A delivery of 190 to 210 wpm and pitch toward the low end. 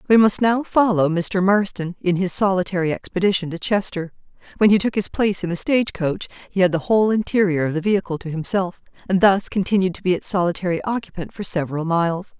No: average, 200 wpm; medium, 185 Hz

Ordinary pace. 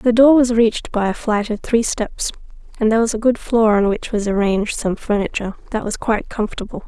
No: fast, 225 wpm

